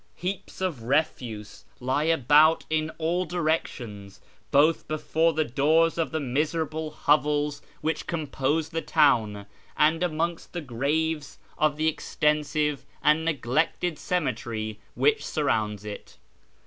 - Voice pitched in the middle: Yes, medium, 150 Hz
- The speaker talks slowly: Yes, slow, 120 wpm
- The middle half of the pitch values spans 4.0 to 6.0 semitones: No, average, 3.1 semitones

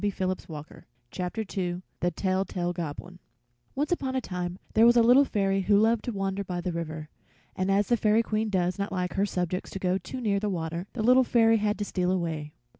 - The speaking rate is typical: No, fast, 225 wpm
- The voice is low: No, high, 195 Hz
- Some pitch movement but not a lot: Yes, average, 3.4 semitones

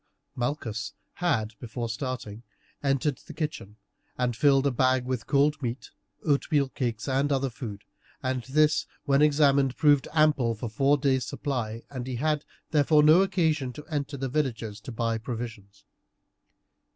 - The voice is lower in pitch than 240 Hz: Yes, low, 135 Hz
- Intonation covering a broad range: No, average, 3.7 semitones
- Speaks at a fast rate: No, average, 150 wpm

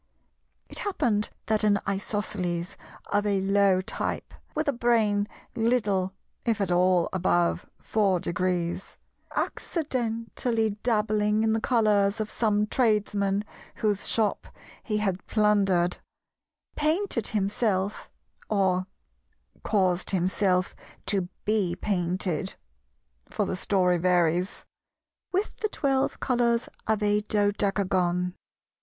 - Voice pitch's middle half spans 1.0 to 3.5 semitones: Yes, average, 3.0 semitones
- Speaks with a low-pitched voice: No, high, 205 Hz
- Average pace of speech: No, slow, 100 wpm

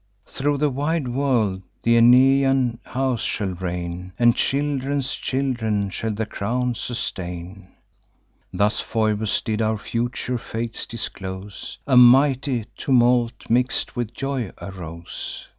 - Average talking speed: No, slow, 115 wpm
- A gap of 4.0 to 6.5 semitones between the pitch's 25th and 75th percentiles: Yes, average, 4.3 semitones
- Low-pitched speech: Yes, low, 120 Hz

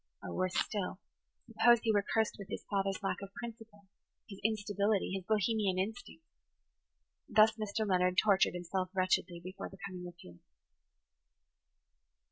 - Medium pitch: No, high, 200 Hz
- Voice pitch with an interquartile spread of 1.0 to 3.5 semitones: Yes, average, 2.8 semitones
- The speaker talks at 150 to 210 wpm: No, average, 140 wpm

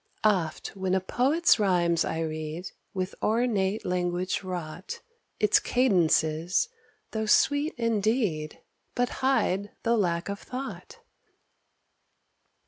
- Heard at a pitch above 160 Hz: Yes, high, 190 Hz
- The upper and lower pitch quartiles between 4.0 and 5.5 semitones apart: Yes, average, 5.0 semitones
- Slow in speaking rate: Yes, slow, 105 wpm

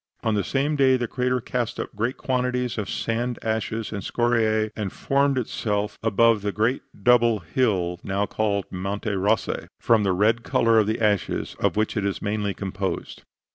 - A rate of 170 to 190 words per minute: Yes, average, 180 wpm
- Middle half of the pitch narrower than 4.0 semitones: Yes, average, 2.9 semitones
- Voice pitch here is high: No, low, 110 Hz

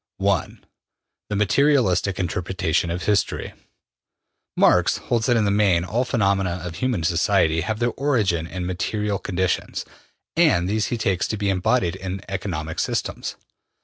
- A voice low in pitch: Yes, very low, 95 Hz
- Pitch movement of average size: Yes, average, 3.5 semitones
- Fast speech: No, average, 145 wpm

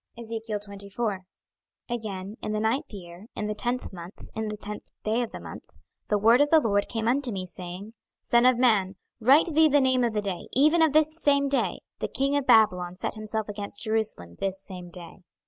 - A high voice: Yes, high, 220 Hz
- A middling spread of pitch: Yes, average, 4.1 semitones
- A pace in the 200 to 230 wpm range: Yes, fast, 205 wpm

